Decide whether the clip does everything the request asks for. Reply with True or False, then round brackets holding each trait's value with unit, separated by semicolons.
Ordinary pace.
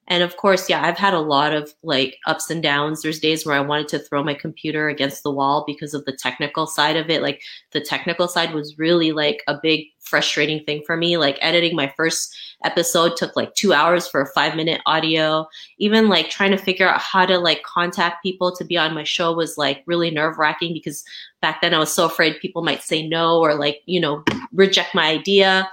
False (230 wpm)